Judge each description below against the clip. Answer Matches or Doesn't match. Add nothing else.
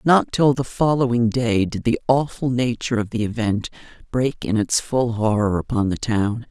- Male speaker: Doesn't match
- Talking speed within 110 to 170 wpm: Doesn't match